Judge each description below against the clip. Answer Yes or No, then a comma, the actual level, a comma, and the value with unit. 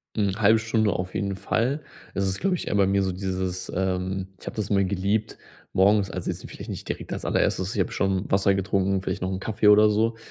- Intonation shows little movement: Yes, narrow, 2.0 semitones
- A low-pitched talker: Yes, low, 100 Hz